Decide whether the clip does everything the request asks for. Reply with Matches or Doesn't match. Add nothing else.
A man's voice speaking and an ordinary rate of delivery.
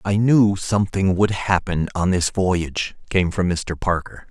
Matches